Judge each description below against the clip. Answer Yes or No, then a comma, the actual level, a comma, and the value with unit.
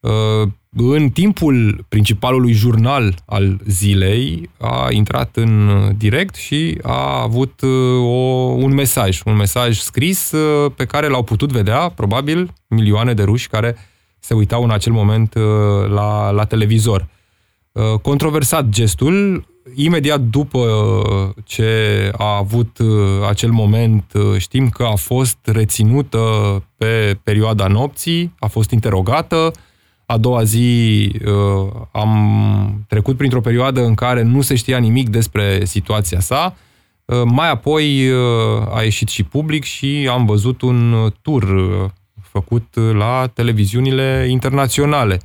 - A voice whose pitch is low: Yes, low, 115 Hz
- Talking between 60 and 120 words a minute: Yes, slow, 115 wpm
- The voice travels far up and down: No, average, 3.7 semitones